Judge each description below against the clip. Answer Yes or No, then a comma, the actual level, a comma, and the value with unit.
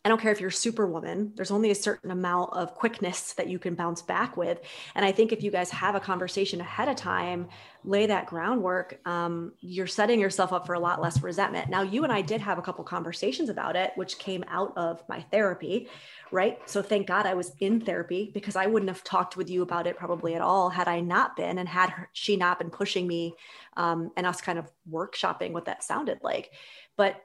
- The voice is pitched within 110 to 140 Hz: No, medium, 185 Hz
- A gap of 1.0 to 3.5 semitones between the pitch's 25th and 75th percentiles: Yes, narrow, 2.4 semitones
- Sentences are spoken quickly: Yes, fast, 225 wpm